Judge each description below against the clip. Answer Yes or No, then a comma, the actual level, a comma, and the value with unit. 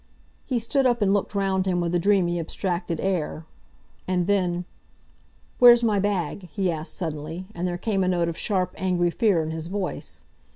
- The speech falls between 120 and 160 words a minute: No, average, 180 wpm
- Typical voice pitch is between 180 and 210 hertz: Yes, medium, 185 Hz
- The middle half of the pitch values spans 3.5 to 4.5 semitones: No, average, 2.7 semitones